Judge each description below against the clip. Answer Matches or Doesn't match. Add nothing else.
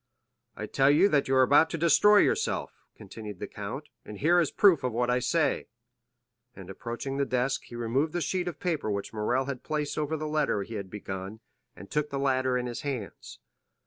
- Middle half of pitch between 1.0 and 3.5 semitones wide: Doesn't match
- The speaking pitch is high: Doesn't match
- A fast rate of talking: Matches